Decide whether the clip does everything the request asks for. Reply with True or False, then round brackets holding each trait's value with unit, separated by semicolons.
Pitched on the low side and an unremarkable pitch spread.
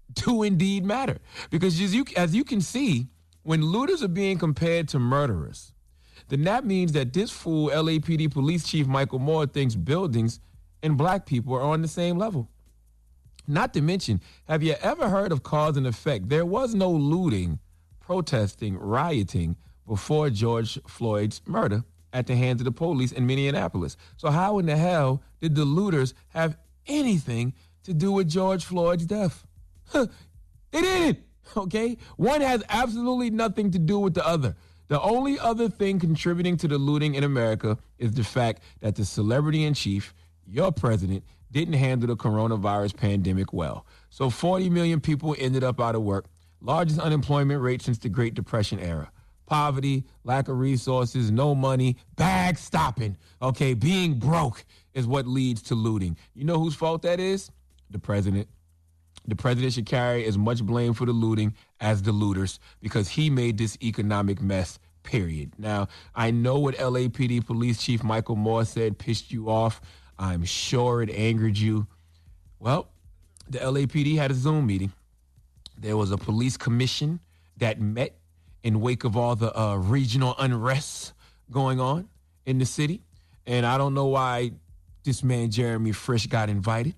False (125 Hz; 6.8 semitones)